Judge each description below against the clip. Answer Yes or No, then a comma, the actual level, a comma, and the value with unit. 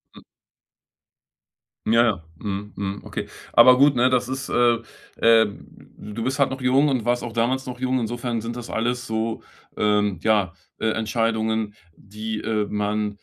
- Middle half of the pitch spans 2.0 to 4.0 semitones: Yes, narrow, 2.6 semitones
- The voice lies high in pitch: No, low, 115 Hz